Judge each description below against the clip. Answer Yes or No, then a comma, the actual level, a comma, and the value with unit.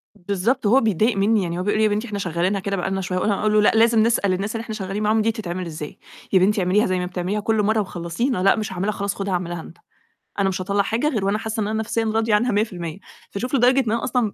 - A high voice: Yes, high, 205 Hz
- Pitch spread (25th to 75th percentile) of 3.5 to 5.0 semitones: No, average, 3.0 semitones